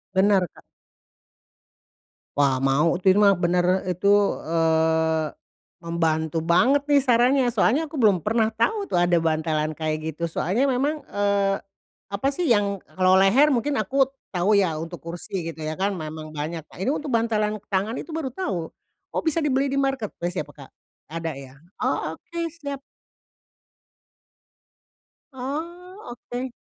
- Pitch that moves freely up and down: Yes, wide, 8.2 semitones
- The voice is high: Yes, high, 195 Hz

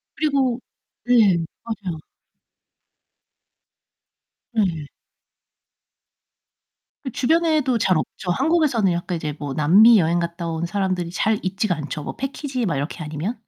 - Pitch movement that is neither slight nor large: No, wide, 6.6 semitones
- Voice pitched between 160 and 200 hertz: Yes, high, 190 Hz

